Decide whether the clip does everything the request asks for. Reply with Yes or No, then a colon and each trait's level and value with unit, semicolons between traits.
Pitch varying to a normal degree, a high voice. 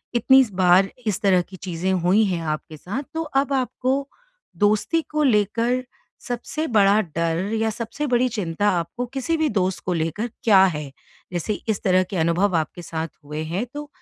No: wide, 5.9 semitones; high, 205 Hz